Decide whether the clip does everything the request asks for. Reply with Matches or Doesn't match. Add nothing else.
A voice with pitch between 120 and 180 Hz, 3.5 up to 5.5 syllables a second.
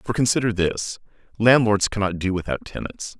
Doesn't match